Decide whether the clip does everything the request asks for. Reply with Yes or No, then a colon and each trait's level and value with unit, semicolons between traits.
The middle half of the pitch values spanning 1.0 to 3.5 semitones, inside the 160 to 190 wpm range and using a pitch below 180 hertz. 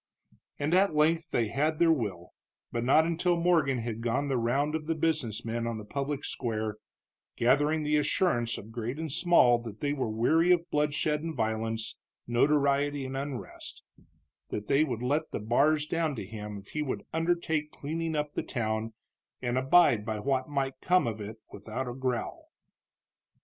No: average, 5.1 semitones; average, 175 wpm; low, 135 Hz